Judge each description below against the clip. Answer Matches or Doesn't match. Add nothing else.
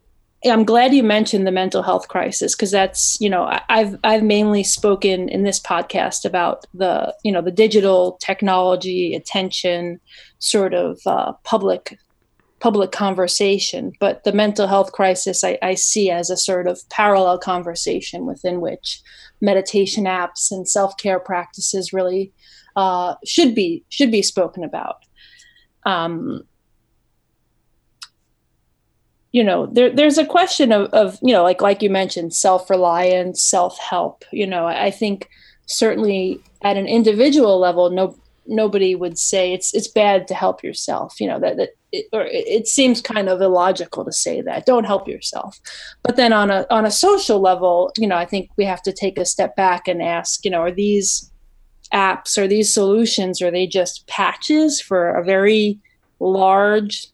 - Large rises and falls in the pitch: Doesn't match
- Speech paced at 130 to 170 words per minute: Matches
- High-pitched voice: Matches